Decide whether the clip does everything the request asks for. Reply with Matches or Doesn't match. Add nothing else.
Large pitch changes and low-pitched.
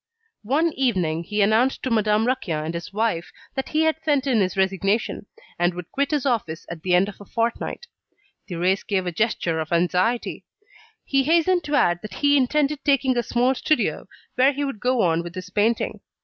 Doesn't match